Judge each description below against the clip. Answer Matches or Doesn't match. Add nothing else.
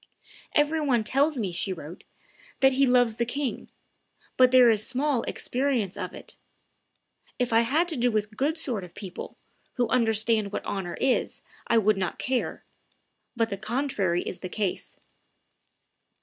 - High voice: Matches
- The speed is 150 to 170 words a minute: Matches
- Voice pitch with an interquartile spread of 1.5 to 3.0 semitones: Doesn't match